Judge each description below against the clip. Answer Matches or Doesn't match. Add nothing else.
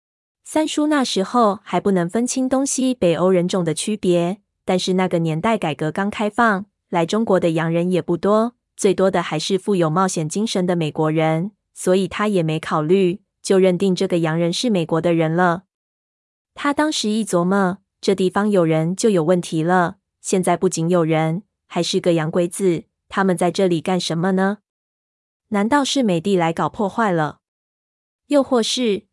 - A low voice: Doesn't match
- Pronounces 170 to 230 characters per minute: Doesn't match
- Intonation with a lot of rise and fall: Doesn't match